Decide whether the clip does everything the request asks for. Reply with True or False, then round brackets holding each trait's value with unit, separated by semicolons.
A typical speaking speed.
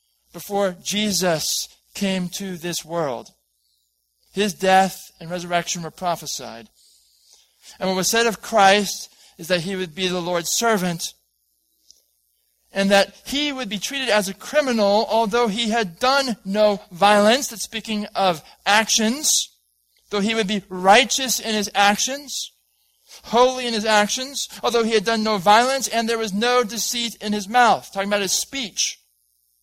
True (150 wpm)